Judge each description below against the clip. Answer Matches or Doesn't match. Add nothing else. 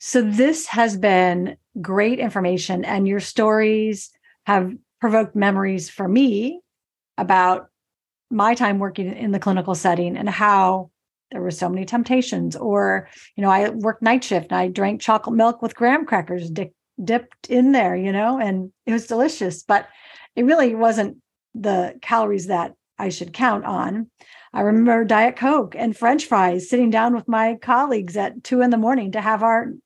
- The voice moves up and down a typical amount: Matches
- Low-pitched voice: Doesn't match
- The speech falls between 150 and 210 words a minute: Matches